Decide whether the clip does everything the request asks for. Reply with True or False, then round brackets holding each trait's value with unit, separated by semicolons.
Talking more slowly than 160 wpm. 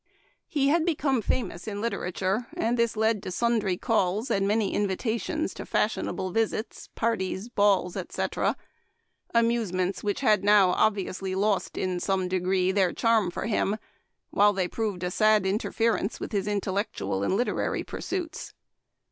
True (150 wpm)